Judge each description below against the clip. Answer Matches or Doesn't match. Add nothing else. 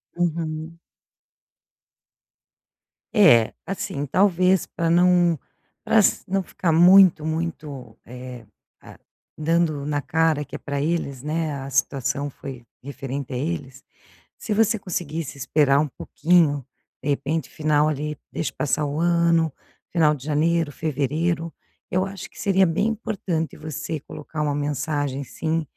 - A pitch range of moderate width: Matches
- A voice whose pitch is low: Doesn't match